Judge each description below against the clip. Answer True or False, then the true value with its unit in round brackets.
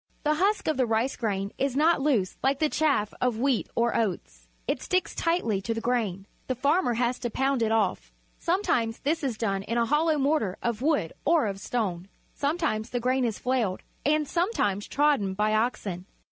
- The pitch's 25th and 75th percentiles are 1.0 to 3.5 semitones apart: False (5.5 semitones)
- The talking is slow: False (195 wpm)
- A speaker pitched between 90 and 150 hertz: False (245 Hz)